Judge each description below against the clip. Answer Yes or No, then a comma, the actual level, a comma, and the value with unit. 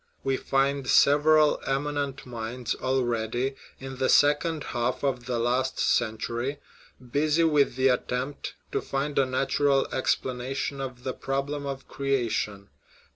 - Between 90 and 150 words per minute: Yes, average, 140 wpm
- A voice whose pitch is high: No, low, 135 Hz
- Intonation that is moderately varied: No, narrow, 2.2 semitones